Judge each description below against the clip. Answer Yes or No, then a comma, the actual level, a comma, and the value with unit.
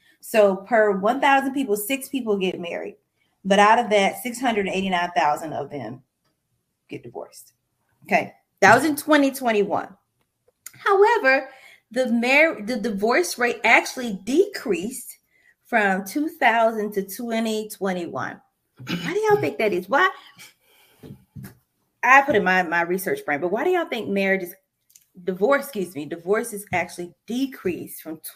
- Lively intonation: Yes, wide, 5.9 semitones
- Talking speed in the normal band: Yes, average, 155 wpm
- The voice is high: Yes, high, 220 Hz